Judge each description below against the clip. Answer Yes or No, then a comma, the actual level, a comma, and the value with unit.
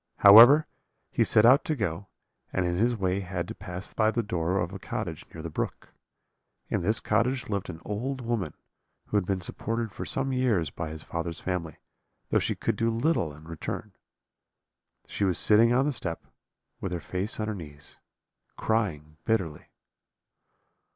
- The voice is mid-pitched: No, low, 100 Hz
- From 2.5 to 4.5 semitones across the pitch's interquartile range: No, average, 5.1 semitones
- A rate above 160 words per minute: Yes, average, 175 wpm